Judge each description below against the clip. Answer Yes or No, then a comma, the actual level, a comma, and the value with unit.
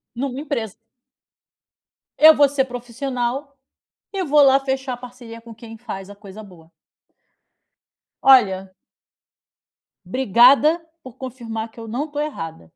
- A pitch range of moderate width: Yes, average, 3.6 semitones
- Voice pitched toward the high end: Yes, high, 245 Hz